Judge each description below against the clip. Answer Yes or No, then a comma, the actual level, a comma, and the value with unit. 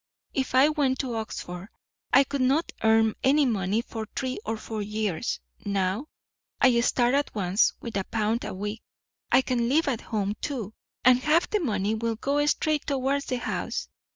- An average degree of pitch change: Yes, average, 4.1 semitones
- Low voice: No, high, 235 Hz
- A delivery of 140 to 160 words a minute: No, average, 180 wpm